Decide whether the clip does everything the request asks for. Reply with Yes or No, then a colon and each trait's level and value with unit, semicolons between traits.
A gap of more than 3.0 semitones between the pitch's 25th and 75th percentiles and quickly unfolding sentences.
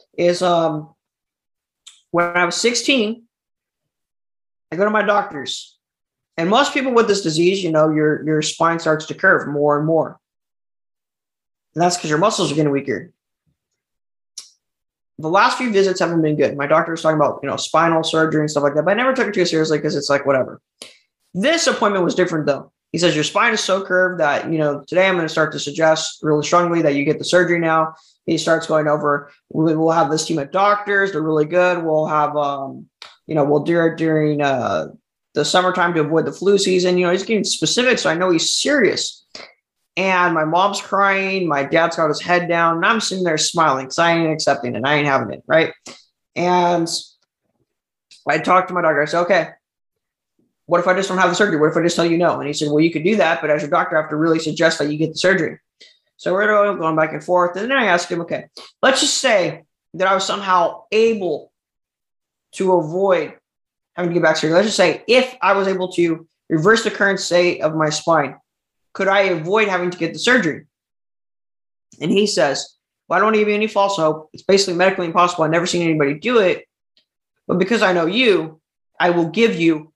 Yes: average, 3.5 semitones; fast, 220 wpm